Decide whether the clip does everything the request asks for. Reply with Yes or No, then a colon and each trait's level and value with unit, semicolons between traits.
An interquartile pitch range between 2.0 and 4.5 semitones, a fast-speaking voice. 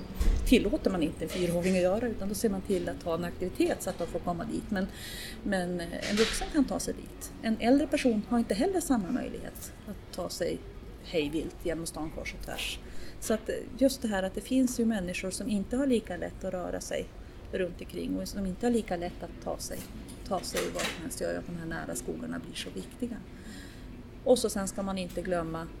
No: average, 5.1 semitones; fast, 225 wpm